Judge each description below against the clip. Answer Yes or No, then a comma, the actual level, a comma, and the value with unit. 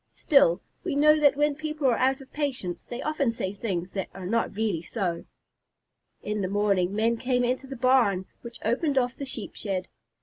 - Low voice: No, high, 235 Hz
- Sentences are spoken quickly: No, average, 195 wpm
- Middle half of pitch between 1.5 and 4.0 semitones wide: No, wide, 5.6 semitones